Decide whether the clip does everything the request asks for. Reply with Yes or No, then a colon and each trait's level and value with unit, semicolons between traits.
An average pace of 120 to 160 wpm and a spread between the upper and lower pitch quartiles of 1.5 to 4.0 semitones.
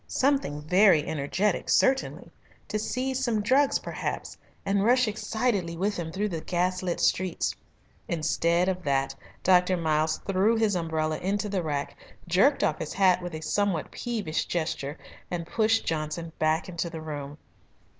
No: average, 150 wpm; average, 4.8 semitones